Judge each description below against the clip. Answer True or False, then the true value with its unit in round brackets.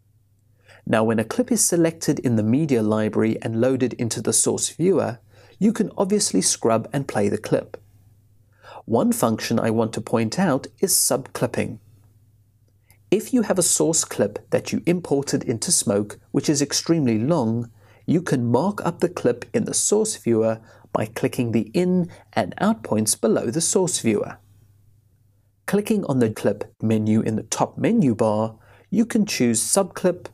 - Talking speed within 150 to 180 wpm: True (165 wpm)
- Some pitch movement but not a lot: False (6.6 semitones)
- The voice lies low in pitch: True (115 Hz)